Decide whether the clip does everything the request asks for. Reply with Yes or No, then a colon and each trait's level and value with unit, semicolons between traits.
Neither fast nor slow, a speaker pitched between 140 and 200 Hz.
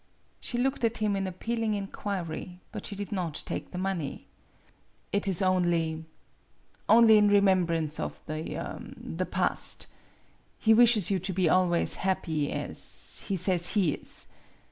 Yes: average, 145 wpm; high, 190 Hz